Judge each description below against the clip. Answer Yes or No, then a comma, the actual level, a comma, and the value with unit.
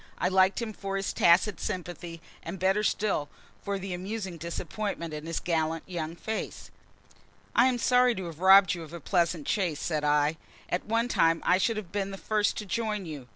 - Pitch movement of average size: Yes, average, 3.8 semitones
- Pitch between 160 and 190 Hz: Yes, medium, 185 Hz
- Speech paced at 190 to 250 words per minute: Yes, average, 200 wpm